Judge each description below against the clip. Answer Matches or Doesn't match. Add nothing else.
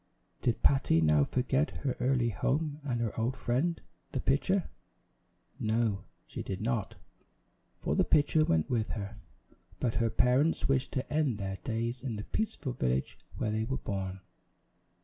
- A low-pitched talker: Matches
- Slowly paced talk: Doesn't match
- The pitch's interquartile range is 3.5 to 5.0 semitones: Matches